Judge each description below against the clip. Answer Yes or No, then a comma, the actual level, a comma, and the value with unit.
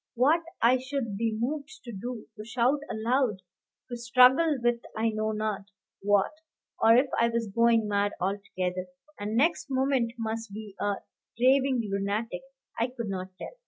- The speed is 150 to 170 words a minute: Yes, average, 160 wpm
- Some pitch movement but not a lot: Yes, average, 3.5 semitones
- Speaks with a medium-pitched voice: No, high, 230 Hz